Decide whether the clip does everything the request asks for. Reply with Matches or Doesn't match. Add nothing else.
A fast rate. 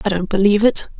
Matches